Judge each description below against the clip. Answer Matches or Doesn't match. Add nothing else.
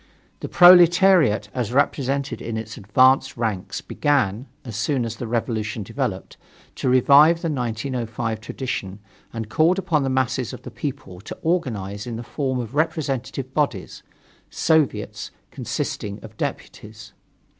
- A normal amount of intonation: Matches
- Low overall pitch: Matches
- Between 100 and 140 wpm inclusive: Matches